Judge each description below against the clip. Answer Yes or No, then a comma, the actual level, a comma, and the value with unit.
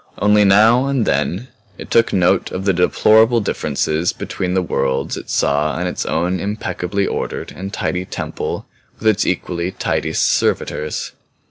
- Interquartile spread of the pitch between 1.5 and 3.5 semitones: Yes, average, 3.2 semitones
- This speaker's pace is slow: No, average, 150 wpm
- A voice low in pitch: Yes, very low, 95 Hz